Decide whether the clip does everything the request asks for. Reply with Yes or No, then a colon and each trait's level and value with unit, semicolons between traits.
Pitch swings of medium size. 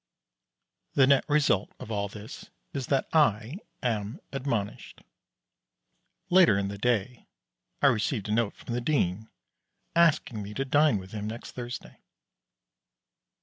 Yes: average, 4.8 semitones